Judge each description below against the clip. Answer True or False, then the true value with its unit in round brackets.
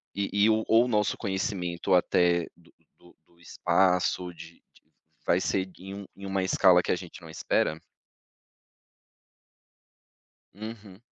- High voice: False (95 Hz)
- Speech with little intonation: True (2.3 semitones)